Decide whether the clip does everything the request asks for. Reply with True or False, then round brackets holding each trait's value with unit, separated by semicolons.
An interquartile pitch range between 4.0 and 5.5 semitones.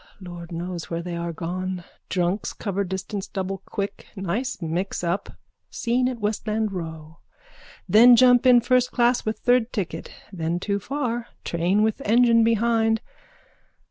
True (4.8 semitones)